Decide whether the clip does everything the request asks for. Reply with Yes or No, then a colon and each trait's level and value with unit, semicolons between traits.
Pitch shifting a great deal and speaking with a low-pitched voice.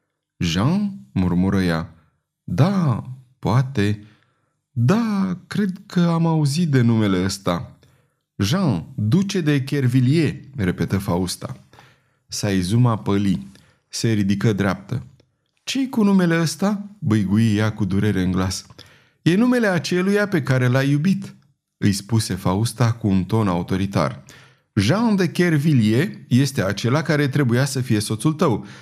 Yes: wide, 8.1 semitones; low, 130 Hz